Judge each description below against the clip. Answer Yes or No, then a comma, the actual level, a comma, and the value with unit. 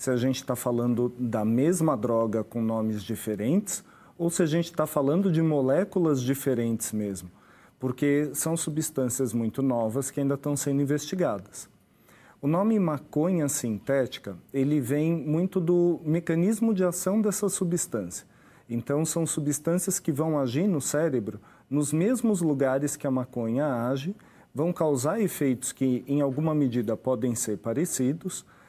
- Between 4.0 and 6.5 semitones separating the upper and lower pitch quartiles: Yes, average, 5.0 semitones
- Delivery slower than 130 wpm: No, average, 145 wpm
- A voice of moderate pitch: Yes, medium, 145 Hz